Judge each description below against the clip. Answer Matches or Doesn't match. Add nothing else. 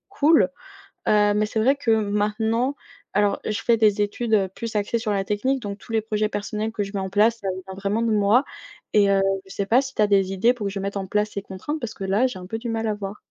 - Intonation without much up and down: Matches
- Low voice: Doesn't match